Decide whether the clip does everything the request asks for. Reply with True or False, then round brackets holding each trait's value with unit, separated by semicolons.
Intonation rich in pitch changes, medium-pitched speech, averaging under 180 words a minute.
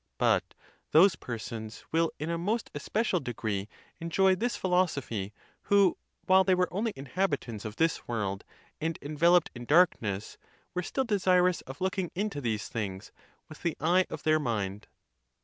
True (7.9 semitones; 160 Hz; 150 wpm)